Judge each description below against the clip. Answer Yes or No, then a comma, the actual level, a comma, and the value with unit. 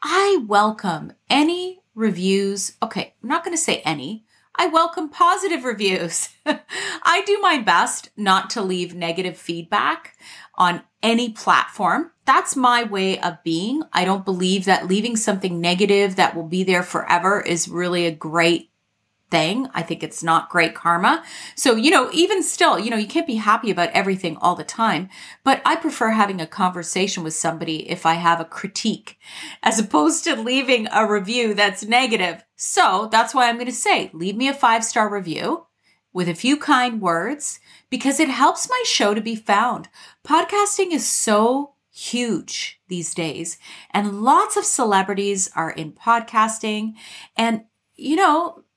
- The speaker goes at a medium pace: Yes, average, 165 wpm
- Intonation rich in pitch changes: Yes, wide, 7.5 semitones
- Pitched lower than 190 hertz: No, high, 215 Hz